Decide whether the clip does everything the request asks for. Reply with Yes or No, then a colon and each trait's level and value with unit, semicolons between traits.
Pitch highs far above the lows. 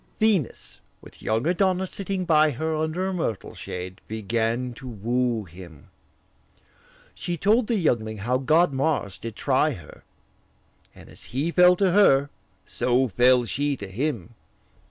Yes: wide, 7.4 semitones